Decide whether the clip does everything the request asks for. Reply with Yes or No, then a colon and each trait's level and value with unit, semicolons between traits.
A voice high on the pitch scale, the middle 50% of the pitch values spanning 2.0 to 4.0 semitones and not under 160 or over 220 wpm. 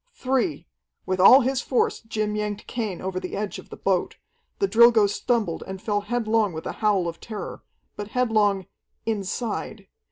Yes: high, 210 Hz; average, 3.1 semitones; average, 165 wpm